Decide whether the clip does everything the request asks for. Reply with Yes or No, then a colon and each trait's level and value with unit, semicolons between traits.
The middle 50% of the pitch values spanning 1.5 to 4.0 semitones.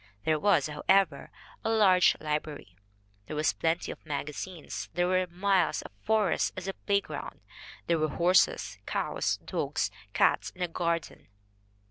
Yes: average, 3.7 semitones